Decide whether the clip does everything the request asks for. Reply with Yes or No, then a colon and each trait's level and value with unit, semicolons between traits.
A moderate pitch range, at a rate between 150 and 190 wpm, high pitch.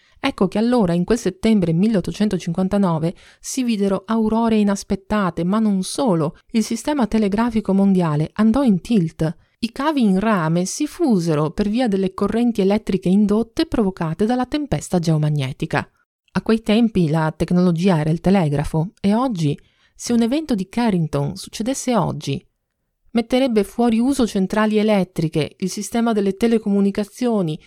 No: average, 4.3 semitones; average, 135 wpm; high, 205 Hz